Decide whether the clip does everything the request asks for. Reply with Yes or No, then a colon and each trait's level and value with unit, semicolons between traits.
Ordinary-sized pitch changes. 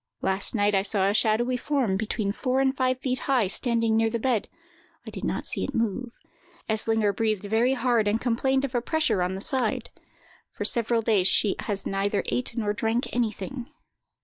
Yes: average, 3.3 semitones